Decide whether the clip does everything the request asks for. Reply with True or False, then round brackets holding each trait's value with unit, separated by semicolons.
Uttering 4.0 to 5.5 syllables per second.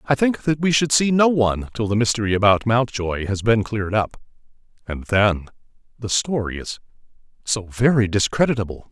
True (5.3 syllables/s)